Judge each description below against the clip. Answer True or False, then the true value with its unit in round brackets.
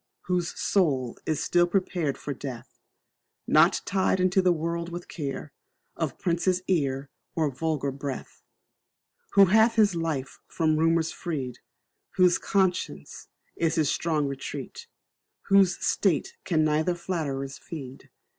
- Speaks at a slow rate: True (125 wpm)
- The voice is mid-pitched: True (165 Hz)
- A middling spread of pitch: True (4.3 semitones)